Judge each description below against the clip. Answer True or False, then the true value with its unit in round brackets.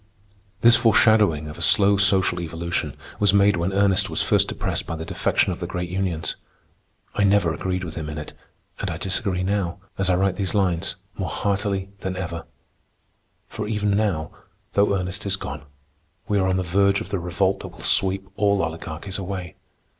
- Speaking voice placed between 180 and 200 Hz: False (95 Hz)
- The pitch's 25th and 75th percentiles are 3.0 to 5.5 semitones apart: False (2.4 semitones)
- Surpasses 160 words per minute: True (185 wpm)